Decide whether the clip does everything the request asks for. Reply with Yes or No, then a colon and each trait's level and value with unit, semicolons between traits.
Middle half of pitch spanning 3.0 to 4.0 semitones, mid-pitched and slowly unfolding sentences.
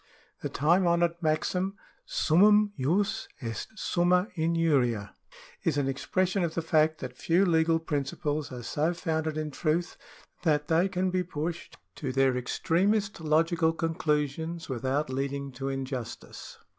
Yes: average, 3.7 semitones; medium, 160 Hz; slow, 130 wpm